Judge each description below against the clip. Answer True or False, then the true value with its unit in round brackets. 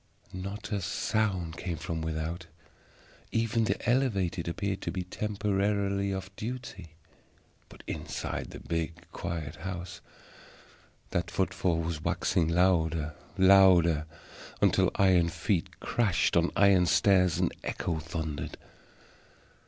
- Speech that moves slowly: True (115 wpm)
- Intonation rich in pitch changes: False (3.1 semitones)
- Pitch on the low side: True (90 Hz)